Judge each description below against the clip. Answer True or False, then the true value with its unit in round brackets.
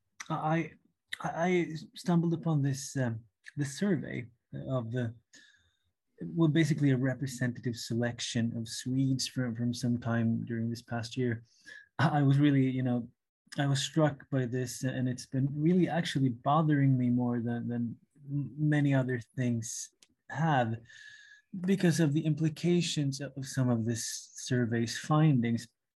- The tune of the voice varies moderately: True (4.4 semitones)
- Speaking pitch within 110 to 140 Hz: True (135 Hz)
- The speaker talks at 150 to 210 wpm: False (135 wpm)